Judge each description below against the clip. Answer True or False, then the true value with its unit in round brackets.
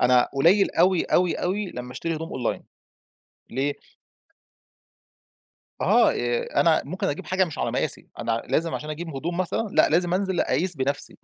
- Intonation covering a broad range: False (5.0 semitones)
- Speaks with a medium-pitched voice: True (165 Hz)